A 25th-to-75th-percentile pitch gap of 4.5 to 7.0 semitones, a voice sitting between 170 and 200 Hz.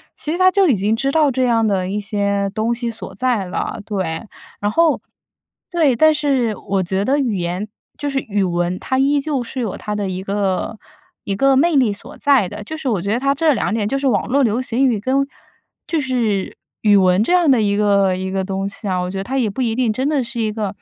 No: wide, 5.4 semitones; high, 225 Hz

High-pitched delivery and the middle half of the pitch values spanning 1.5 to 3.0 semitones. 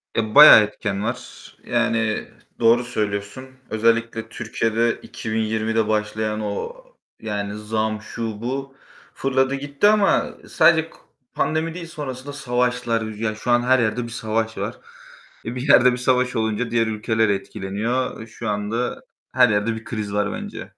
No: low, 115 Hz; narrow, 2.5 semitones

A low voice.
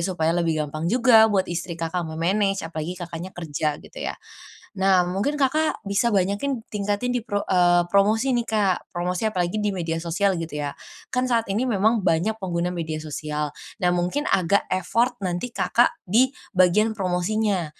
No: medium, 185 Hz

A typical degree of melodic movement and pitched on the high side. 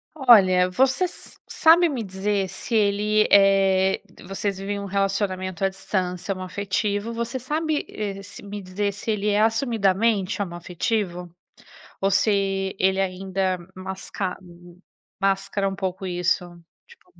No: narrow, 2.0 semitones; high, 195 Hz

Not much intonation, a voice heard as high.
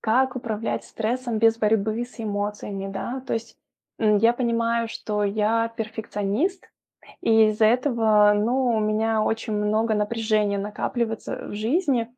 Yes: narrow, 1.8 semitones; high, 220 Hz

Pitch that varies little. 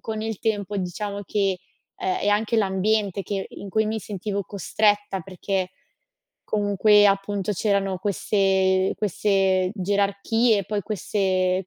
Yes: narrow, 1.7 semitones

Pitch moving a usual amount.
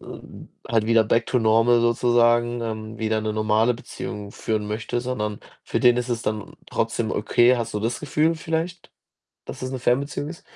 No: narrow, 2.1 semitones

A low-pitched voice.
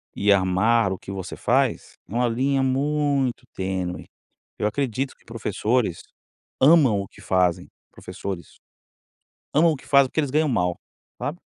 Yes: low, 120 Hz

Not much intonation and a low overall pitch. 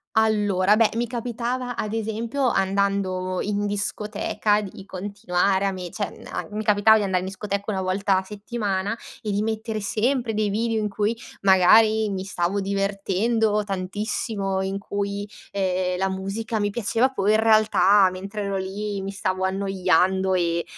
No: narrow, 2.2 semitones; high, 200 Hz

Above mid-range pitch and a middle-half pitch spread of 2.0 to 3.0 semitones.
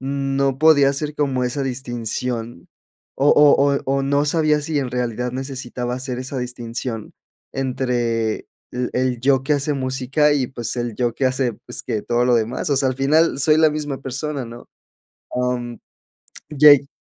No: low, 130 Hz; narrow, 2.4 semitones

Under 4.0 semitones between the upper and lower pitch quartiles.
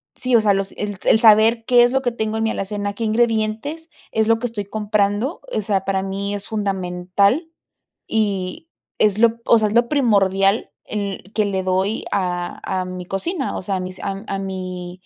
Yes: average, 2.8 semitones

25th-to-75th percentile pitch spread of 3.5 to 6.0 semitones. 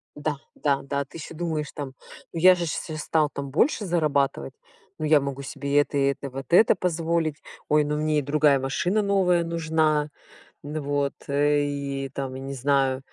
No: narrow, 2.5 semitones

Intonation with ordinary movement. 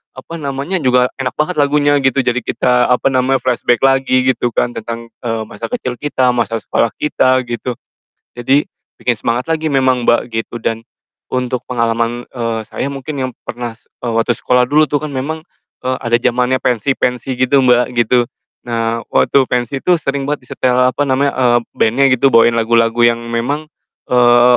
No: narrow, 2.3 semitones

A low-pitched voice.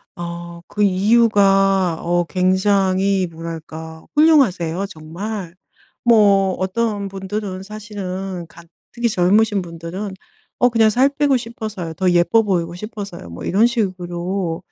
No: high, 195 Hz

